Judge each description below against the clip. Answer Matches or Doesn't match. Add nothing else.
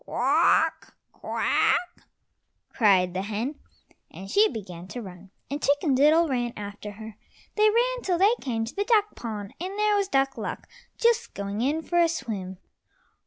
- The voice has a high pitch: Matches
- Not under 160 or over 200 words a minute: Matches